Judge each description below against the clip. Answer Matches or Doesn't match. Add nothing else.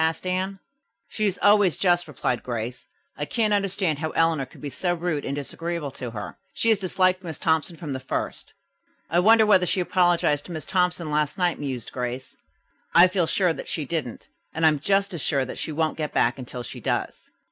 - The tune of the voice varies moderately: Matches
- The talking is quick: Matches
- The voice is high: Doesn't match